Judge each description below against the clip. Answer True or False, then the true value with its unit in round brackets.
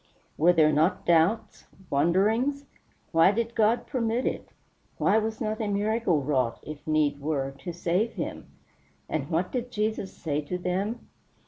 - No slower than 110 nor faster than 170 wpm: True (150 wpm)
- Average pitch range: False (6.2 semitones)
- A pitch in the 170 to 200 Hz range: True (185 Hz)